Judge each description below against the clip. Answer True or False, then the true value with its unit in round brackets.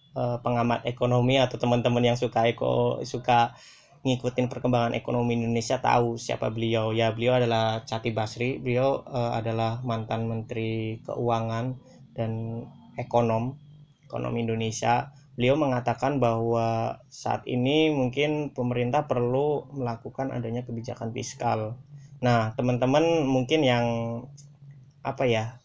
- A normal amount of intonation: False (2.1 semitones)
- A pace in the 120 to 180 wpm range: False (110 wpm)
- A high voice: False (120 Hz)